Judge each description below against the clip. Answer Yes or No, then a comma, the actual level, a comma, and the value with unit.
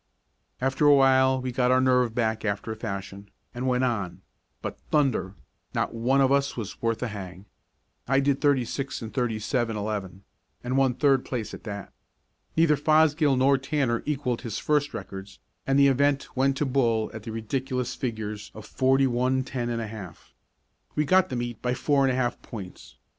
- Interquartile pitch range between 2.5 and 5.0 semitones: Yes, average, 3.5 semitones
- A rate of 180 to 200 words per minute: Yes, average, 190 wpm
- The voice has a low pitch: Yes, low, 125 Hz